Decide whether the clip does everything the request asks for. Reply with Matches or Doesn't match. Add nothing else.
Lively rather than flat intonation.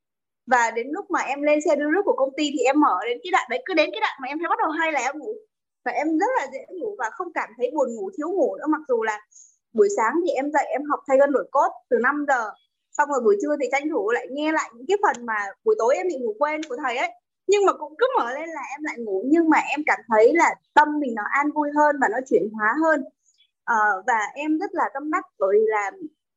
Matches